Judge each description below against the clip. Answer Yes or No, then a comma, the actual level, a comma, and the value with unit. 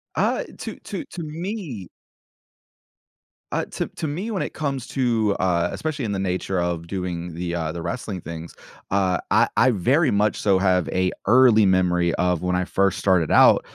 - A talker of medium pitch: No, very low, 95 Hz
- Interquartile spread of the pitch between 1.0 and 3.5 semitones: No, wide, 6.3 semitones